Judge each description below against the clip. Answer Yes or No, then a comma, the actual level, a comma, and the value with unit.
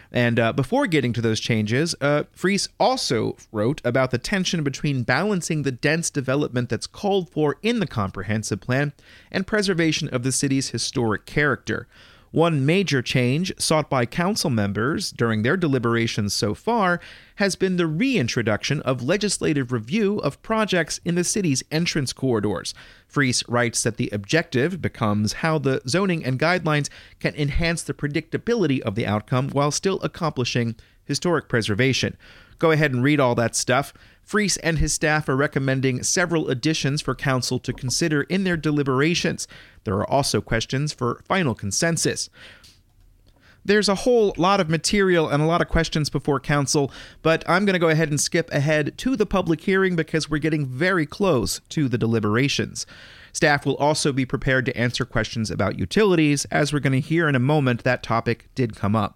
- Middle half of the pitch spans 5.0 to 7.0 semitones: Yes, wide, 5.5 semitones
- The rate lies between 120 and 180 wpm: Yes, average, 170 wpm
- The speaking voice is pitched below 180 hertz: Yes, medium, 140 Hz